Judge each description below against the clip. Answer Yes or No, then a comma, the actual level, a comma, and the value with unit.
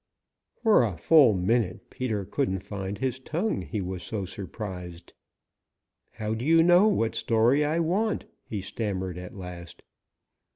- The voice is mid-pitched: No, low, 110 Hz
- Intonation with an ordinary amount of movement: No, wide, 7.1 semitones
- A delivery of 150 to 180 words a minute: No, average, 140 wpm